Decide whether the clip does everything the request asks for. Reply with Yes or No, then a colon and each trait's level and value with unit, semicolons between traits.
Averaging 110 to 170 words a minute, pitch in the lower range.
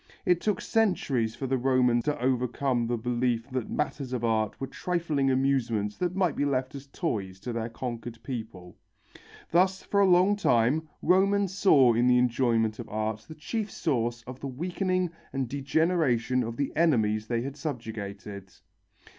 Yes: average, 165 wpm; low, 130 Hz